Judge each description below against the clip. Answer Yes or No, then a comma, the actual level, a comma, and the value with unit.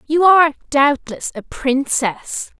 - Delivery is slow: Yes, slow, 115 wpm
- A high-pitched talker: Yes, very high, 285 Hz